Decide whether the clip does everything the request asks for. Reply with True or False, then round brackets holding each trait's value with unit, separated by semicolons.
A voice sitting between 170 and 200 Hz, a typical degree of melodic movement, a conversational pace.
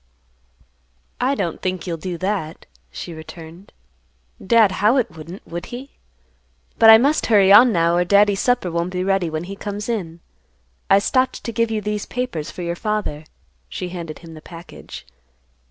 True (190 Hz; 4.1 semitones; 170 wpm)